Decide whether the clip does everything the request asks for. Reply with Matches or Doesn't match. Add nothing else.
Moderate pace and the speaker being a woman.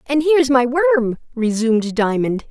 Matches